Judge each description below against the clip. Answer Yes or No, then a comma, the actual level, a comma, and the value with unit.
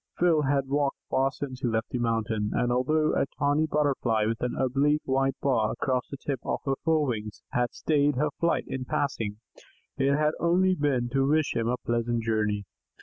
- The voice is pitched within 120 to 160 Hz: Yes, low, 135 Hz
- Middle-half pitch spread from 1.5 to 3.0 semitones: No, average, 3.8 semitones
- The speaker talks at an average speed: Yes, average, 190 wpm